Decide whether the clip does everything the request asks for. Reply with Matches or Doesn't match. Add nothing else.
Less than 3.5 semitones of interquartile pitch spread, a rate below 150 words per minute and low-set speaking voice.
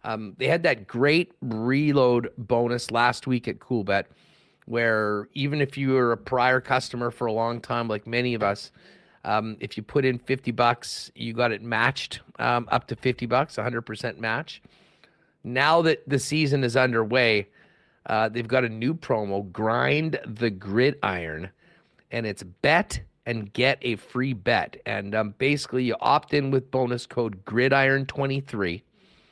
Doesn't match